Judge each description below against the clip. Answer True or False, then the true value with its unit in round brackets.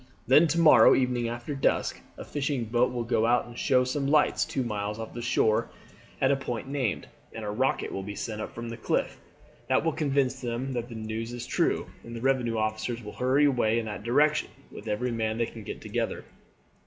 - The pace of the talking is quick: True (215 wpm)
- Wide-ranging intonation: False (3.0 semitones)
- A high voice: False (120 Hz)